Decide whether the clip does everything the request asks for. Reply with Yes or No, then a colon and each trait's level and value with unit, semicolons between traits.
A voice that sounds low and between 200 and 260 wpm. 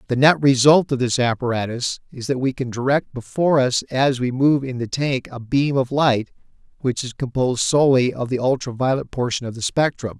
Yes: low, 130 Hz; fast, 205 wpm